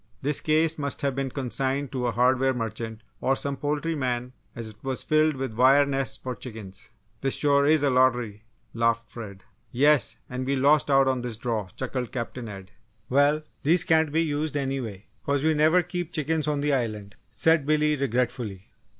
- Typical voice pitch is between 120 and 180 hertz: Yes, low, 135 Hz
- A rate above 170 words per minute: Yes, average, 185 wpm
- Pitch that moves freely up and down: No, average, 3.7 semitones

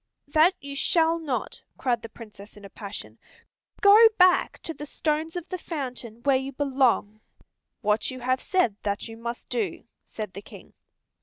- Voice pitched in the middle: No, very high, 260 Hz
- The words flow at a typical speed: Yes, average, 170 wpm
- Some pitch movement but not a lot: No, wide, 6.7 semitones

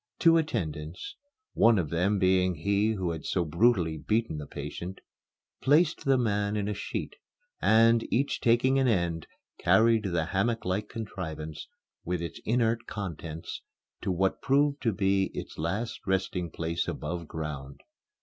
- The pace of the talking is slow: No, average, 145 wpm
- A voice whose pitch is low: Yes, very low, 95 Hz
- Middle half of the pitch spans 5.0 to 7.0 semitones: Yes, average, 5.3 semitones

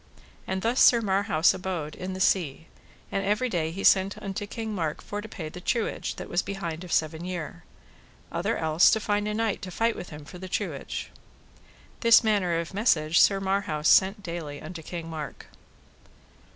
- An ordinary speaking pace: Yes, average, 185 wpm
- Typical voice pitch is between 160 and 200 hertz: Yes, medium, 185 Hz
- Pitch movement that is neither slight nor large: Yes, average, 4.0 semitones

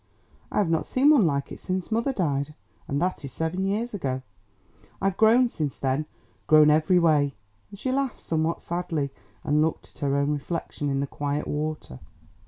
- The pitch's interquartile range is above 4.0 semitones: Yes, average, 5.1 semitones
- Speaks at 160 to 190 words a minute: Yes, average, 185 wpm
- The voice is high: No, medium, 160 Hz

